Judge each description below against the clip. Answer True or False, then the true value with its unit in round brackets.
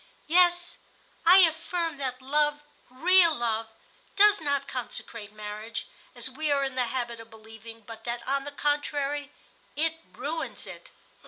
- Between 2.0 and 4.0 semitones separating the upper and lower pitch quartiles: False (5.0 semitones)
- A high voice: True (275 Hz)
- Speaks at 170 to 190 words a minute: False (145 wpm)